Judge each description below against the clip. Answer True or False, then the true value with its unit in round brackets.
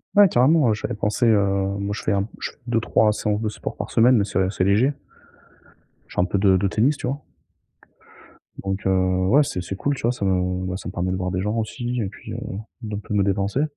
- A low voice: True (105 Hz)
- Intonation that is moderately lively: True (3.6 semitones)